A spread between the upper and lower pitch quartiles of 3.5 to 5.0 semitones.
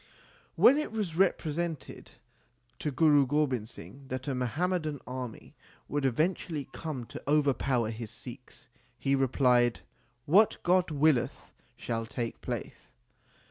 Yes: average, 4.1 semitones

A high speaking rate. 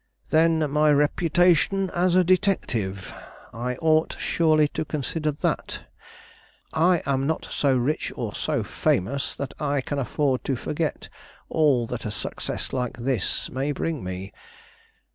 No: average, 140 wpm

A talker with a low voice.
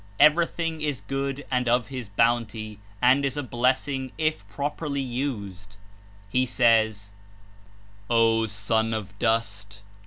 Yes: low, 120 Hz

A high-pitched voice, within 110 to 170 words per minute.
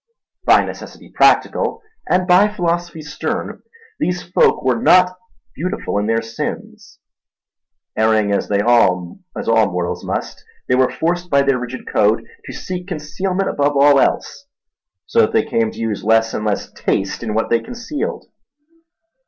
No: medium, 140 Hz; average, 145 wpm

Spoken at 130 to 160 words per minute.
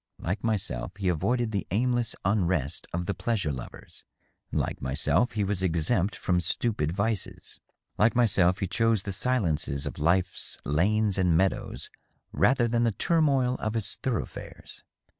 Yes: average, 150 wpm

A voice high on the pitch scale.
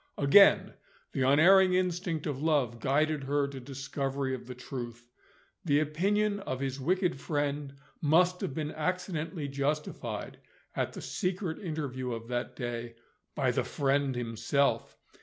No: medium, 145 Hz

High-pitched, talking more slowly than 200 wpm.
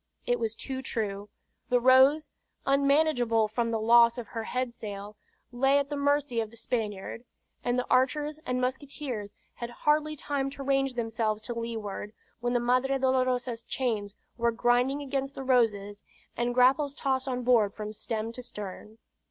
Yes: high, 245 Hz; average, 165 wpm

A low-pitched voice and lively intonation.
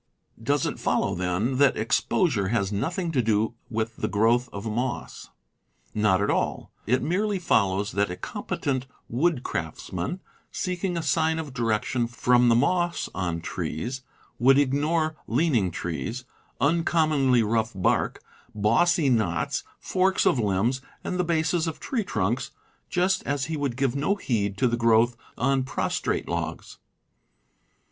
Yes: low, 125 Hz; wide, 6.7 semitones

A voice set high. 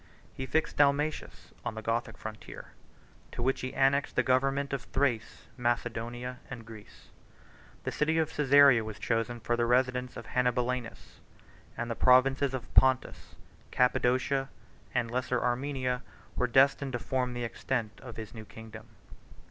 No: low, 125 Hz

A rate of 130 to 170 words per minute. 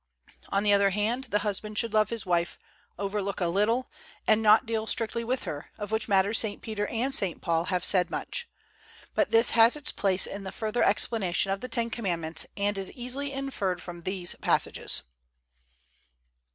No: average, 180 wpm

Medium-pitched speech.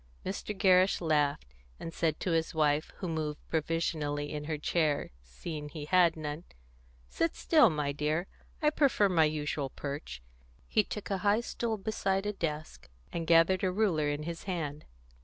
Yes: medium, 160 Hz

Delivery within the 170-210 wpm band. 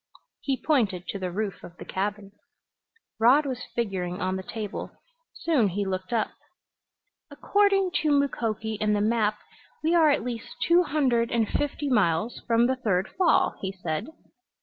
No: average, 160 wpm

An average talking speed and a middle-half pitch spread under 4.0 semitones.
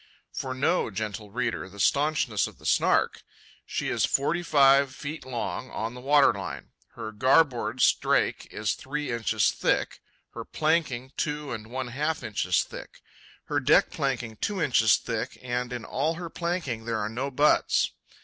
No: average, 160 wpm; average, 4.7 semitones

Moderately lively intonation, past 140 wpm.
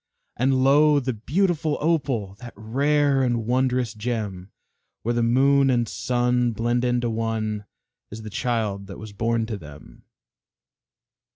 No: average, 3.3 semitones; slow, 135 wpm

